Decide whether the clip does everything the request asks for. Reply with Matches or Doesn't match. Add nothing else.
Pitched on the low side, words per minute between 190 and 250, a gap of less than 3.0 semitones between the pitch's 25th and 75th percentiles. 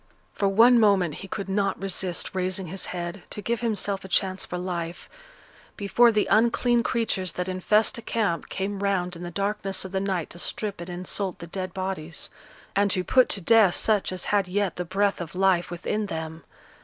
Doesn't match